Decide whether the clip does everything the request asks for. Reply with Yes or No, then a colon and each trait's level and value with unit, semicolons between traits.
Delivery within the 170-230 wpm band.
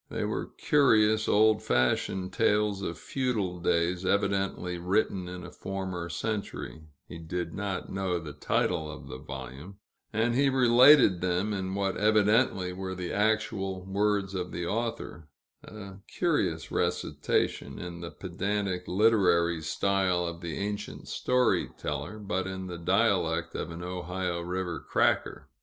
No: average, 140 wpm